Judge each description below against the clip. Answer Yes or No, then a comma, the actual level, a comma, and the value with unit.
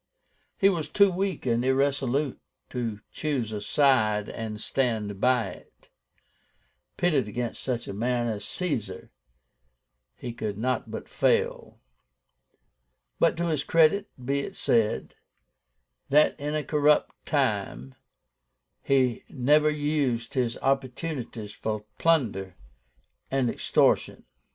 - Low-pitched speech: Yes, low, 130 Hz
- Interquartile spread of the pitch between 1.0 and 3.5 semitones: No, average, 4.9 semitones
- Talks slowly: Yes, slow, 115 wpm